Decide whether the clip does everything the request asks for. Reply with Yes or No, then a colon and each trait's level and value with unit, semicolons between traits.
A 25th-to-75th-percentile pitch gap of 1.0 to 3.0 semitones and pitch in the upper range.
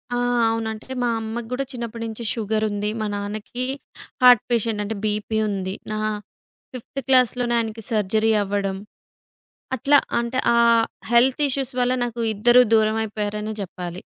Yes: narrow, 2.4 semitones; high, 220 Hz